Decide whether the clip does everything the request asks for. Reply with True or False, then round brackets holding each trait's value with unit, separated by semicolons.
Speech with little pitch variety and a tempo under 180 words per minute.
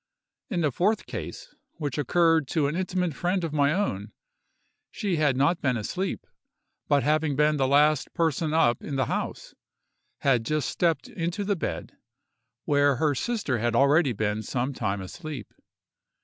False (4.3 semitones; 160 wpm)